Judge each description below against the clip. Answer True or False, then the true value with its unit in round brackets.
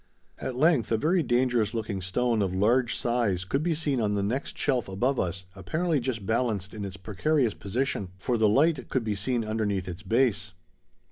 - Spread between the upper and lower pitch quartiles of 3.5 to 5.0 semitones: True (4.7 semitones)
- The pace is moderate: True (190 wpm)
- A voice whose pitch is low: True (115 Hz)